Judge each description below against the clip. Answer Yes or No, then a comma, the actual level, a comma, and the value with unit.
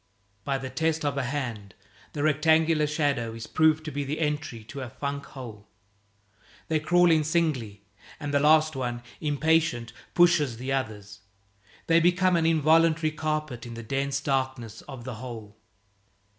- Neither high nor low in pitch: Yes, medium, 145 Hz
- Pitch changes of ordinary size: Yes, average, 4.5 semitones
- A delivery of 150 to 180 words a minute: Yes, average, 155 wpm